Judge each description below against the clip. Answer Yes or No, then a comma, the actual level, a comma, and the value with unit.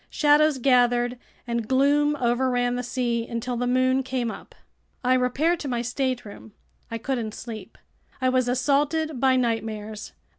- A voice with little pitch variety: Yes, narrow, 2.0 semitones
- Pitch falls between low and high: No, very high, 250 Hz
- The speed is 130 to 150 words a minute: Yes, average, 145 wpm